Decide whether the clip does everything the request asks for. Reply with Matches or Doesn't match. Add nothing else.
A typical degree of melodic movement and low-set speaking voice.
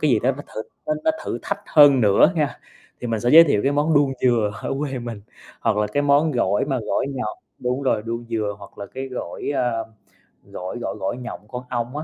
Matches